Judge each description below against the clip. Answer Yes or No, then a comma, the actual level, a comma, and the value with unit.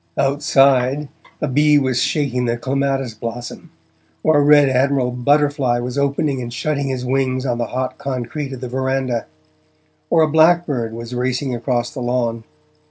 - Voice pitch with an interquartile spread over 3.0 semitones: No, narrow, 2.5 semitones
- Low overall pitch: Yes, low, 130 Hz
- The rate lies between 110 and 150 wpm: No, average, 160 wpm